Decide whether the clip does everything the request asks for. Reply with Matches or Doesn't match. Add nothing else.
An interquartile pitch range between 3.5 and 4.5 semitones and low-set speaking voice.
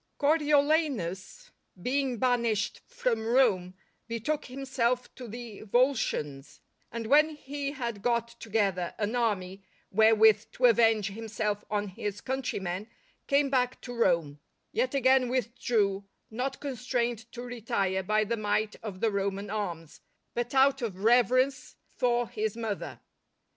Doesn't match